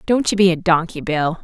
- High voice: No, medium, 175 Hz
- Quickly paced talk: Yes, fast, 250 wpm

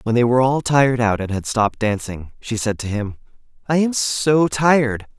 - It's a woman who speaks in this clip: No, male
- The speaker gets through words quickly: Yes, fast, 210 wpm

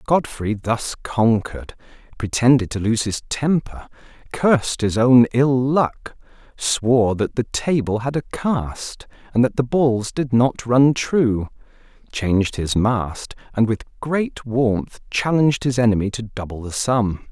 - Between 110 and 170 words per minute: Yes, average, 145 wpm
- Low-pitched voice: Yes, low, 120 Hz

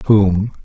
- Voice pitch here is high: No, low, 100 Hz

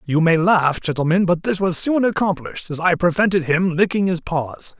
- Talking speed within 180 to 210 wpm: Yes, average, 200 wpm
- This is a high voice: No, medium, 175 Hz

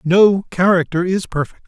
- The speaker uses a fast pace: No, average, 145 wpm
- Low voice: No, medium, 180 Hz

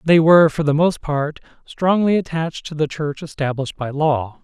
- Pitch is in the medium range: Yes, medium, 155 Hz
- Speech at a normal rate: Yes, average, 190 wpm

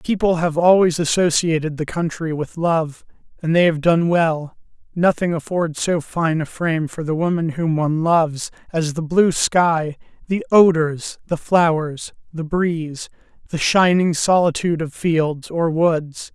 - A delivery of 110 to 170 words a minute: Yes, average, 155 wpm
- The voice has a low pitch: No, medium, 165 Hz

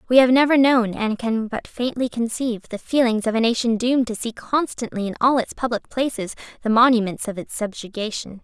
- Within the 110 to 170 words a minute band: No, average, 200 wpm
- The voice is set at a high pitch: Yes, high, 235 Hz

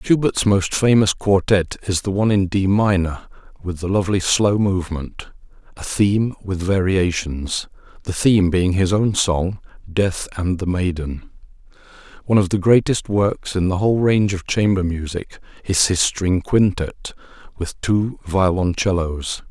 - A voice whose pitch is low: Yes, very low, 95 Hz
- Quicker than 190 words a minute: No, average, 150 wpm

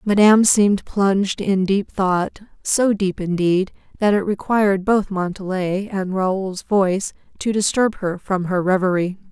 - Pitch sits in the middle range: No, high, 195 Hz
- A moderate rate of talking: Yes, average, 150 wpm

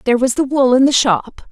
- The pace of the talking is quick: Yes, fast, 275 wpm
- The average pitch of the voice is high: Yes, very high, 255 Hz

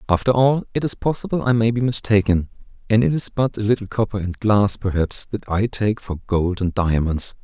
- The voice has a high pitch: No, low, 110 Hz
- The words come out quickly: Yes, fast, 210 wpm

